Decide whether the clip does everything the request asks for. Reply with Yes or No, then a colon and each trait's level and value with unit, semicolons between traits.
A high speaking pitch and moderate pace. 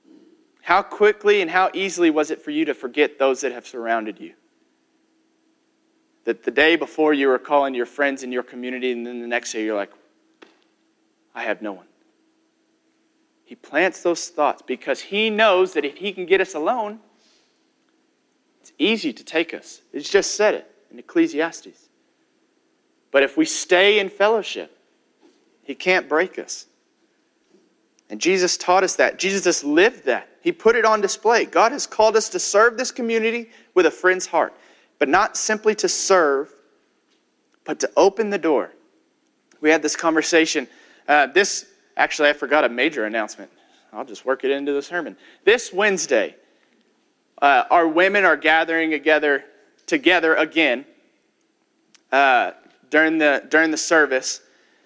Yes: high, 210 Hz; average, 160 wpm